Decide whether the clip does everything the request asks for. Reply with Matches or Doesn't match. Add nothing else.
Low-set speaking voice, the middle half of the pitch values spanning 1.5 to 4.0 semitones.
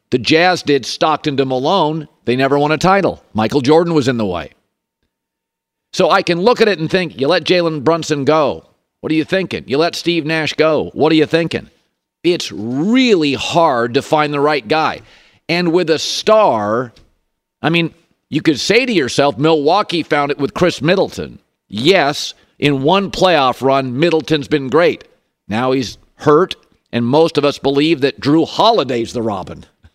Doesn't match